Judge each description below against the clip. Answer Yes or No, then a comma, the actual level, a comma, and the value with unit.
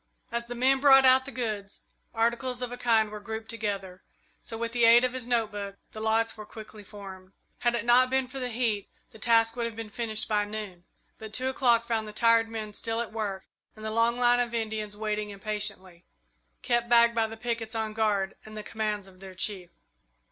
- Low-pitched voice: No, high, 225 Hz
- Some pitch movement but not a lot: No, narrow, 2.1 semitones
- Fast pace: Yes, fast, 215 wpm